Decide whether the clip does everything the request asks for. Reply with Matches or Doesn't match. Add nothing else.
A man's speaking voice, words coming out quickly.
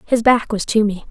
Doesn't match